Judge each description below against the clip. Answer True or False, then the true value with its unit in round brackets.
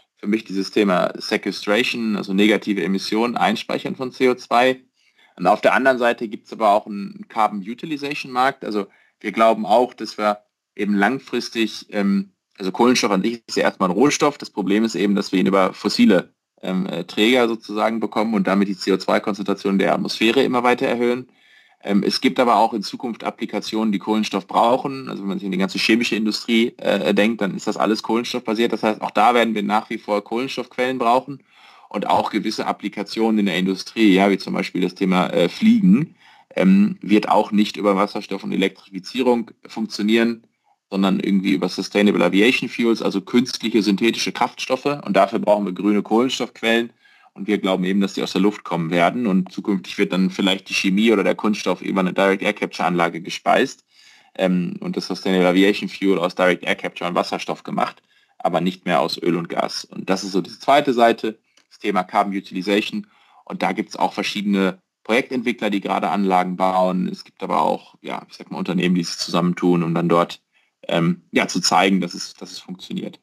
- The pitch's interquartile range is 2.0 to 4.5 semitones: True (3.3 semitones)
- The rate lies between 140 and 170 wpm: False (190 wpm)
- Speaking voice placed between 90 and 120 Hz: True (105 Hz)